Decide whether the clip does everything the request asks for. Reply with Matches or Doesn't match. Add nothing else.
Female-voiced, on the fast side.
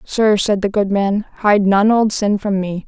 Matches